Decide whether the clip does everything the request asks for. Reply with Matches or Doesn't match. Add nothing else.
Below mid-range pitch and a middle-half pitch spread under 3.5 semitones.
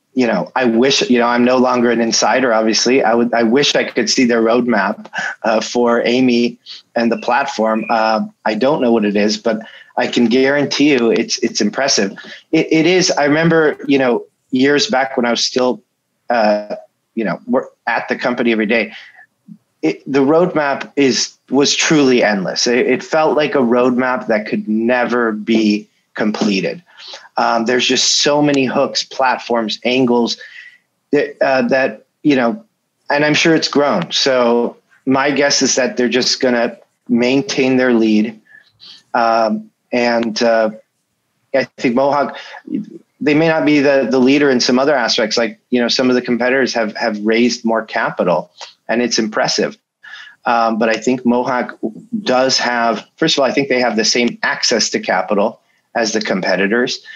Matches